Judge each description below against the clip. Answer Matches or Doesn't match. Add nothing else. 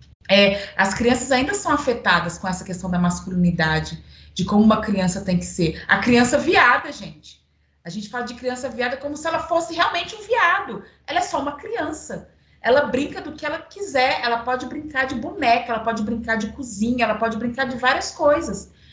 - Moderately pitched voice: Doesn't match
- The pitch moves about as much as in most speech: Doesn't match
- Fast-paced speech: Matches